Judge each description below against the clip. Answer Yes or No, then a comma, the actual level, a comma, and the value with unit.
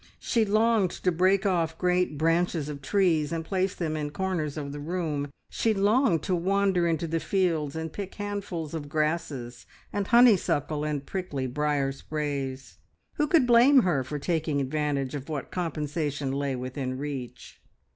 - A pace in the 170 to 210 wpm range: No, average, 160 wpm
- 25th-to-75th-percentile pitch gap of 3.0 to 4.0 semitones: No, average, 4.5 semitones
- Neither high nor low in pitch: Yes, medium, 160 Hz